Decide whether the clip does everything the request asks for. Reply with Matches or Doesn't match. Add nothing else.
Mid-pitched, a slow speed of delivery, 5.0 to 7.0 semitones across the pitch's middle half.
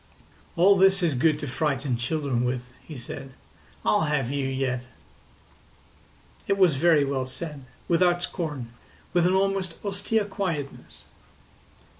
Matches